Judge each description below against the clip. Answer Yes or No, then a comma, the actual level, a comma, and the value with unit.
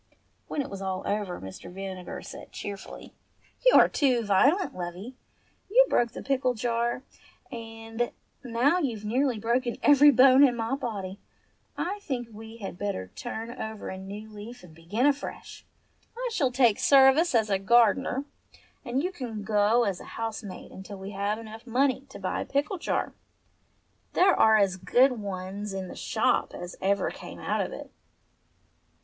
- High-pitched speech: Yes, high, 225 Hz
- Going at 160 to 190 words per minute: Yes, average, 165 wpm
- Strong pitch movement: No, average, 4.6 semitones